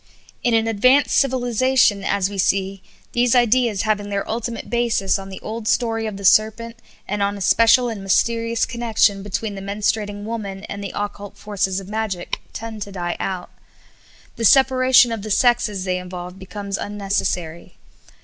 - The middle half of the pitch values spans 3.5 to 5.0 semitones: No, average, 2.8 semitones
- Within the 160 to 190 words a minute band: Yes, average, 165 wpm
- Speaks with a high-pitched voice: Yes, high, 210 Hz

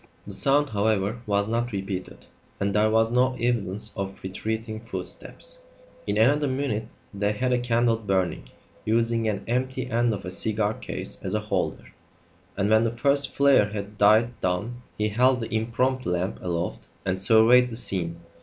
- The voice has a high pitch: No, low, 110 Hz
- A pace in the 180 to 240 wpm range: No, average, 165 wpm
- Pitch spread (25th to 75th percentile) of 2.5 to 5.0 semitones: Yes, average, 3.2 semitones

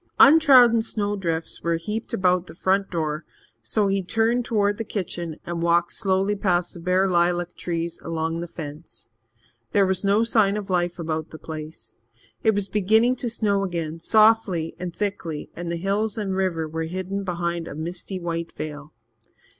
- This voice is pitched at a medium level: Yes, medium, 180 Hz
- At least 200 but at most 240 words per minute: No, average, 170 wpm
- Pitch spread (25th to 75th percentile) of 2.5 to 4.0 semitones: Yes, average, 3.4 semitones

